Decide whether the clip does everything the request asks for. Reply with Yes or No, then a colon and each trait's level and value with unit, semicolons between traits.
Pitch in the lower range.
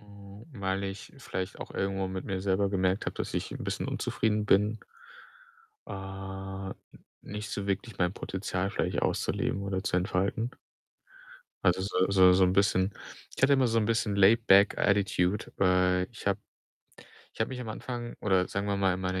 Yes: low, 100 Hz